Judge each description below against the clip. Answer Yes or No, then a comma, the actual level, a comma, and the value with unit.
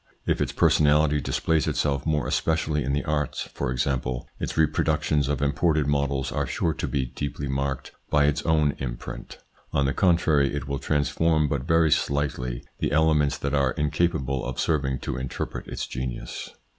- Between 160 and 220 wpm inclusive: Yes, average, 170 wpm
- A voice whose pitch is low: Yes, very low, 70 Hz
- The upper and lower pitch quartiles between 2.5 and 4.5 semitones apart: No, narrow, 2.1 semitones